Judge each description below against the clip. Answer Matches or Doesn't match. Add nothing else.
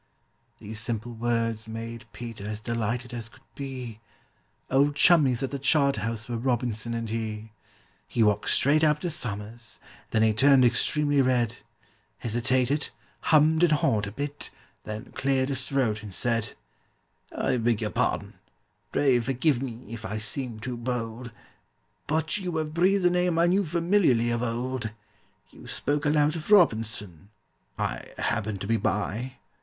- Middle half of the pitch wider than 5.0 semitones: Doesn't match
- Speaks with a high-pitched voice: Doesn't match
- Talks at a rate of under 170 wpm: Matches